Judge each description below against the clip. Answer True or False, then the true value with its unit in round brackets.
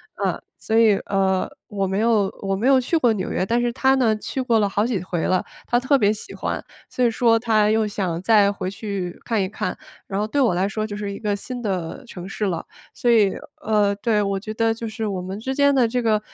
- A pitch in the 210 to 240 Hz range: True (215 Hz)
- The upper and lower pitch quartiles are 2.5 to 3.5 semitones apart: True (3.0 semitones)